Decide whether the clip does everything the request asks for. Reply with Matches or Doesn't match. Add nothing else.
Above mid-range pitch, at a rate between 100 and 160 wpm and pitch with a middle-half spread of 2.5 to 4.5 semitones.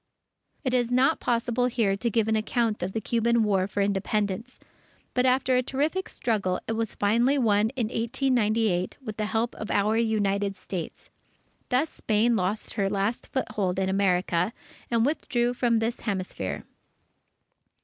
Matches